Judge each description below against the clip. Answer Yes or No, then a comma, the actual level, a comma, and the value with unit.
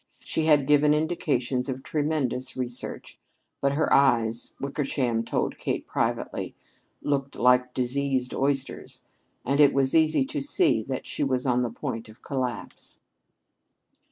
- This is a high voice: No, low, 135 Hz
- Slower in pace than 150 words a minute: Yes, slow, 135 wpm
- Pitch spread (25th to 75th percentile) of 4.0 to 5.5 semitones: No, narrow, 2.6 semitones